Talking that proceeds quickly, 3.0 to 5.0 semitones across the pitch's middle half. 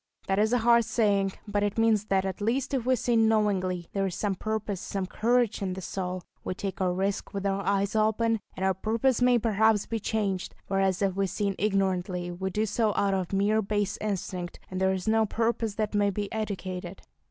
No: fast, 215 wpm; narrow, 2.4 semitones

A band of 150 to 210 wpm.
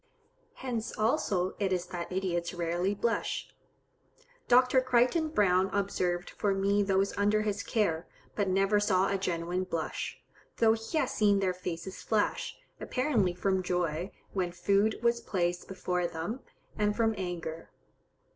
No: average, 140 wpm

